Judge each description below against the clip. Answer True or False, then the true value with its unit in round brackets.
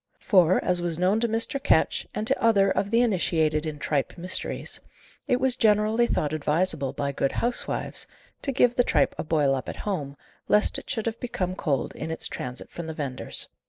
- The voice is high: False (180 Hz)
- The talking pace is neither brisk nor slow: True (195 wpm)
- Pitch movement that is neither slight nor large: False (6.7 semitones)